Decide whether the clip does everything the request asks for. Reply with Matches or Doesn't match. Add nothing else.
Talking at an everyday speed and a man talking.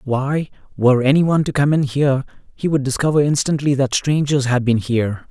Matches